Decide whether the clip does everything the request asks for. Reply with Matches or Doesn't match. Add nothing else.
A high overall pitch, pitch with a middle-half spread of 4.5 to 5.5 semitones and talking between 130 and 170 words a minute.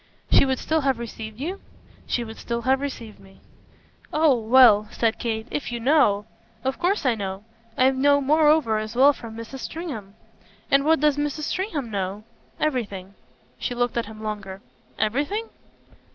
Matches